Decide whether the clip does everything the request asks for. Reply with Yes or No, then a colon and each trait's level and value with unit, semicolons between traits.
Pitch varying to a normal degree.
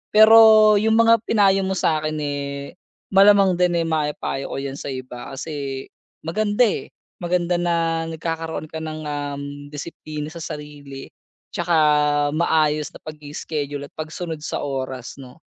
Yes: average, 3.5 semitones